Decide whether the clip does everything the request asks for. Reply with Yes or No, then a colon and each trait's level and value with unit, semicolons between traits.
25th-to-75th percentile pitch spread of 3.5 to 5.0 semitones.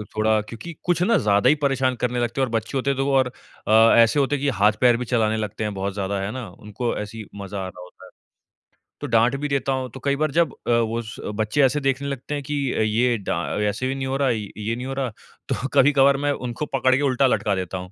Yes: average, 4.1 semitones